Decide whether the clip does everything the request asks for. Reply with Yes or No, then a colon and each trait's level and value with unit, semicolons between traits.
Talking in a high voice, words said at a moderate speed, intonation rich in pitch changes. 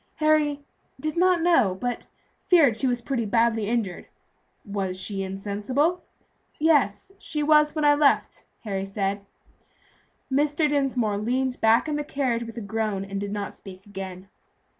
Yes: high, 235 Hz; average, 150 wpm; wide, 6.5 semitones